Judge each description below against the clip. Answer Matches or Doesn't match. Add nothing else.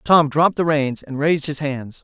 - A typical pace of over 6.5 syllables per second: Doesn't match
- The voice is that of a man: Matches